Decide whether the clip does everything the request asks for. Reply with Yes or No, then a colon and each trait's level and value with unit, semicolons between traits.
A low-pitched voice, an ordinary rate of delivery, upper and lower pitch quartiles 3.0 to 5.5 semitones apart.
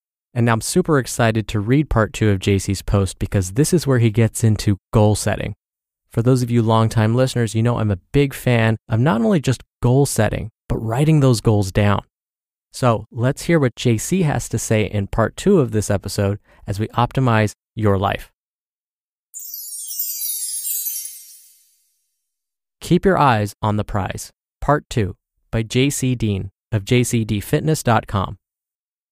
Yes: low, 115 Hz; average, 155 wpm; average, 3.7 semitones